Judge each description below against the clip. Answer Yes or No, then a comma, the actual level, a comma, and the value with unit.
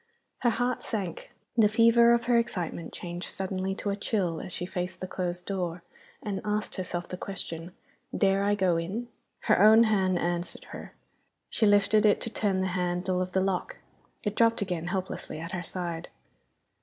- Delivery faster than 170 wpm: Yes, average, 180 wpm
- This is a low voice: No, high, 190 Hz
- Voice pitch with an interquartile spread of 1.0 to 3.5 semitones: Yes, average, 3.0 semitones